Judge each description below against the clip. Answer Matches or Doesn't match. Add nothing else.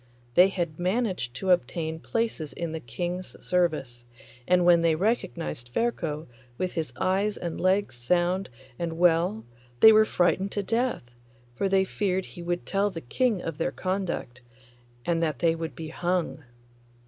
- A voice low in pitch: Doesn't match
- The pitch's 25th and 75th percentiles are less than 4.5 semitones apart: Matches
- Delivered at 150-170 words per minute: Matches